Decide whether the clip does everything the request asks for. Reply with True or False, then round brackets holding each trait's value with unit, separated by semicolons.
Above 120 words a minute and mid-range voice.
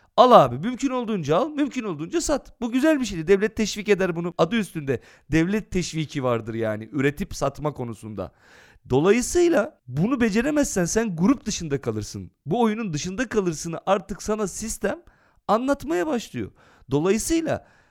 False (140 wpm; 200 Hz)